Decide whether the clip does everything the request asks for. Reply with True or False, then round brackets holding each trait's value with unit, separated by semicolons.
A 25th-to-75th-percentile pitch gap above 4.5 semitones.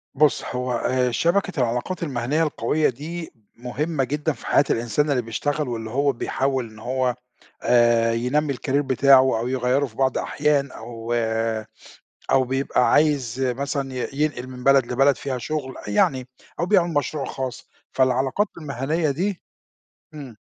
False (3.1 semitones)